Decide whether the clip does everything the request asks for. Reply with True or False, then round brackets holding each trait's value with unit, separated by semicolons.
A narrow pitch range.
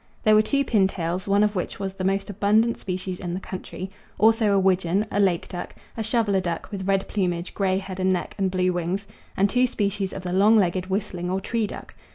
True (2.0 semitones)